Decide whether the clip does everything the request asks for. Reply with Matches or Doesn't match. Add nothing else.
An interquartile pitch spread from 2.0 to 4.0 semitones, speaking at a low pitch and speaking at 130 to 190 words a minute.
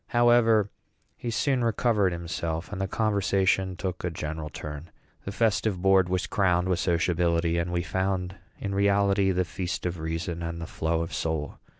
Matches